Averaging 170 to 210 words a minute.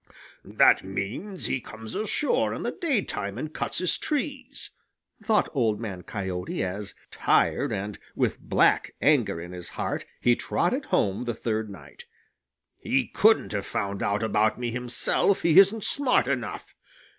No: average, 155 wpm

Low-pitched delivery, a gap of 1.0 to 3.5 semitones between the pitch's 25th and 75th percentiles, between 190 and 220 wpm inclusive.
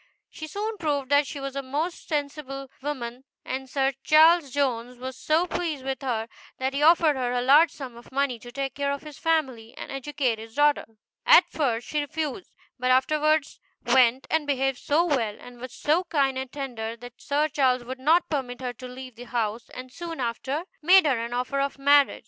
No: very high, 275 Hz; average, 3.2 semitones; average, 200 wpm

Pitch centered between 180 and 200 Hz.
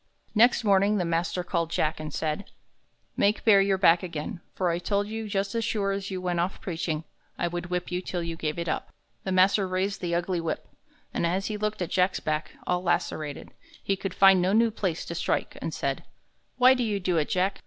Yes: medium, 185 Hz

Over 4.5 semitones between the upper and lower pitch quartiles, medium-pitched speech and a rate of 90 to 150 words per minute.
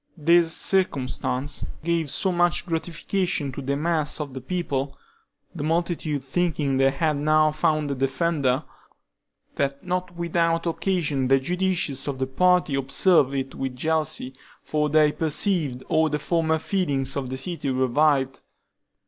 No: average, 3.9 semitones; medium, 150 Hz; average, 140 wpm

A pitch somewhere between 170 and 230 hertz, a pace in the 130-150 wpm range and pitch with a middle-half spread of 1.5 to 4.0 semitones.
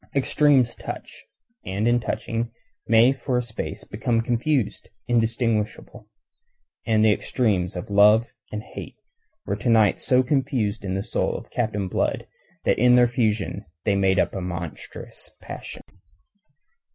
No: low, 115 Hz; average, 140 wpm; average, 3.2 semitones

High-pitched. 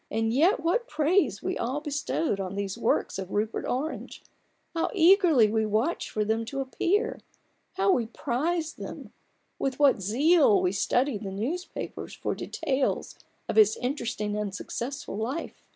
Yes: very high, 260 Hz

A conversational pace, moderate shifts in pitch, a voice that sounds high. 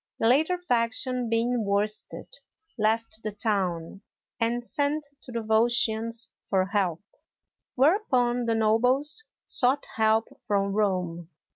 No: slow, 115 wpm; average, 3.0 semitones; high, 225 Hz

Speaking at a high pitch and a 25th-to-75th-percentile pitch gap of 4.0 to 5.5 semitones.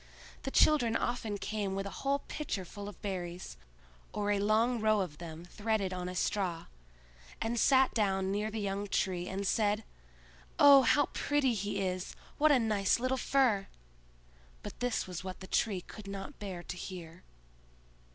No: high, 205 Hz; average, 3.6 semitones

